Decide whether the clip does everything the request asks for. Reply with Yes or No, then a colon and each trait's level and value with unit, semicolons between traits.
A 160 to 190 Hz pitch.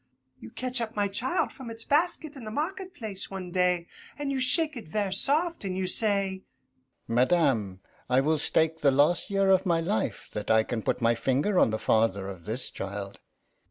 Yes: medium, 185 Hz